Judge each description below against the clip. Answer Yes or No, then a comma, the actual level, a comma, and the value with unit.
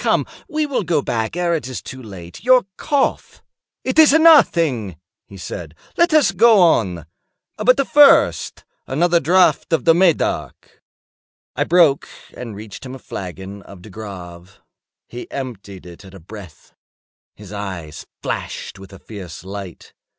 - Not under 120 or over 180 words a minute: Yes, average, 150 wpm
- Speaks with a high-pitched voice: No, low, 120 Hz